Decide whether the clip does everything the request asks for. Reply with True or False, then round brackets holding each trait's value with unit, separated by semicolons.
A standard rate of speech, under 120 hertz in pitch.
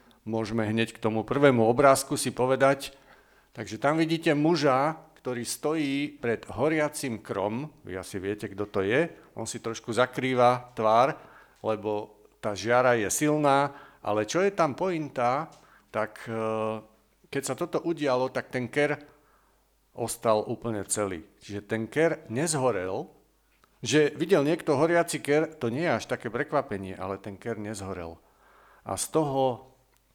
False (140 wpm; 125 Hz)